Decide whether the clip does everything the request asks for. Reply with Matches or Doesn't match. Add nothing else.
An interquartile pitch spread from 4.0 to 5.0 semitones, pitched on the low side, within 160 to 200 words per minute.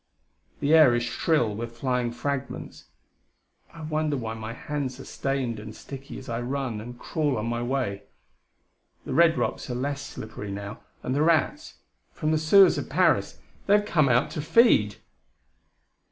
Matches